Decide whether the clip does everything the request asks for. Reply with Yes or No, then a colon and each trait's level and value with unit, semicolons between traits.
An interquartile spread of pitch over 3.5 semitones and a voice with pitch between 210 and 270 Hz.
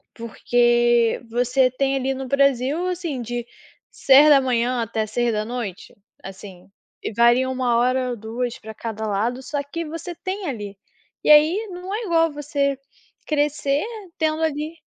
Yes: average, 4.1 semitones; very high, 255 Hz